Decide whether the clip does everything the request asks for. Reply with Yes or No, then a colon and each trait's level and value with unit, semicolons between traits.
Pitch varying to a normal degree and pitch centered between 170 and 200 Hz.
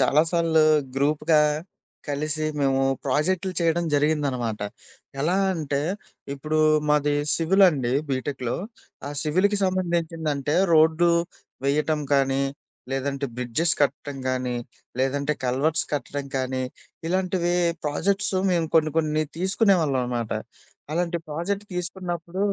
No: average, 3.7 semitones; medium, 155 Hz